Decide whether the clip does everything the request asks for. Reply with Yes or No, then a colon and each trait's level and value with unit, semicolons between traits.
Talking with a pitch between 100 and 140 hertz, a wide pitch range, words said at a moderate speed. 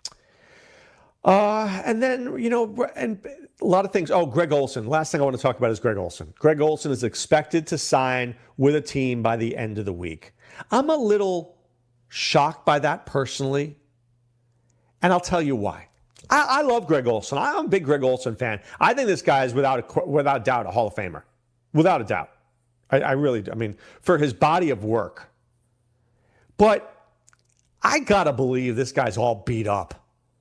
Yes: low, 135 Hz; wide, 6.4 semitones; average, 195 wpm